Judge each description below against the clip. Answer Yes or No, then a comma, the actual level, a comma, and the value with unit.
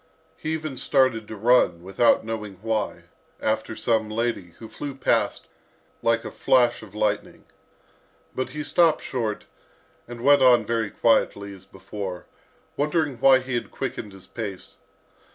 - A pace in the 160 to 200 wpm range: No, average, 145 wpm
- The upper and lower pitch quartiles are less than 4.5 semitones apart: Yes, average, 3.6 semitones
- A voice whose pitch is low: Yes, low, 115 Hz